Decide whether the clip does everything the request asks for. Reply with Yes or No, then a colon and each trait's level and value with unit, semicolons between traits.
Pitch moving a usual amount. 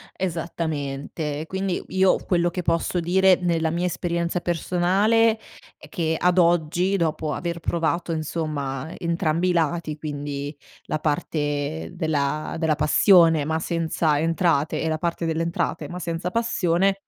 No: narrow, 2.3 semitones